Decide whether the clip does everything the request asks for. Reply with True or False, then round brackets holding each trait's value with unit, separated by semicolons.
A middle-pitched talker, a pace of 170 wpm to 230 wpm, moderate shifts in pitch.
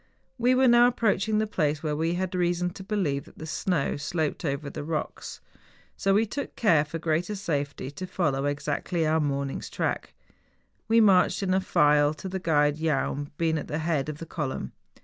True (160 Hz; 190 wpm; 4.4 semitones)